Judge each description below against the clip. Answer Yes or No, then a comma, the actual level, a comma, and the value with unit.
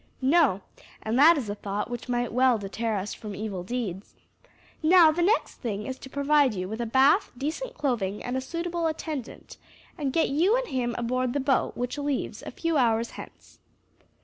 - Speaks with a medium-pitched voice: No, very high, 255 Hz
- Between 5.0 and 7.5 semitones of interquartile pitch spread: Yes, wide, 5.4 semitones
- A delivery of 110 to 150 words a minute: No, average, 185 wpm